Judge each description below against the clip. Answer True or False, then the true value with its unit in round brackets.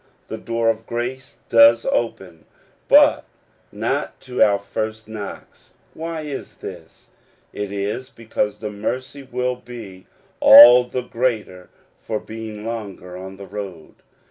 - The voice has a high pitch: False (115 Hz)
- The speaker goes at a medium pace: False (130 wpm)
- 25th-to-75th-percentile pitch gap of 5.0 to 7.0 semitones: False (3.4 semitones)